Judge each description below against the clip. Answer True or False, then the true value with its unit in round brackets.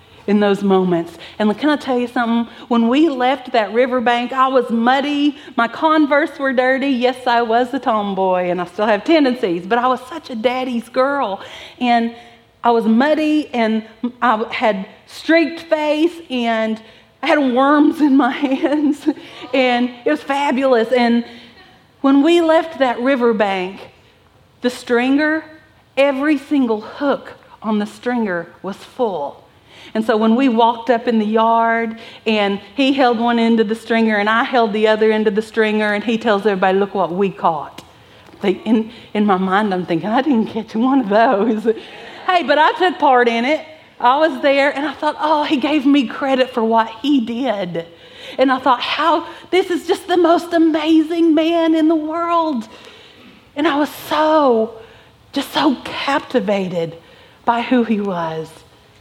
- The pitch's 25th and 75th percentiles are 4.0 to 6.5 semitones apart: True (4.8 semitones)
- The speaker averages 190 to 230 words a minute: False (170 wpm)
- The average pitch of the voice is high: True (245 Hz)